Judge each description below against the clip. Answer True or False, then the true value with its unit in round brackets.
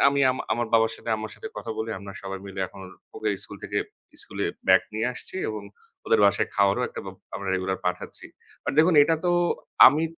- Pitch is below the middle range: True (110 Hz)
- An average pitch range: True (4.1 semitones)